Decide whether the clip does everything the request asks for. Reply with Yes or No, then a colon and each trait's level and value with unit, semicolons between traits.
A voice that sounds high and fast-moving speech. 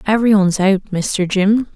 No: high, 200 Hz; average, 170 wpm